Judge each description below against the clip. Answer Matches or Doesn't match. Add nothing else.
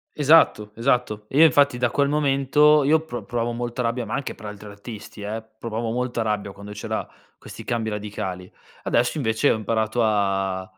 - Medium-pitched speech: Doesn't match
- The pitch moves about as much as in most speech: Matches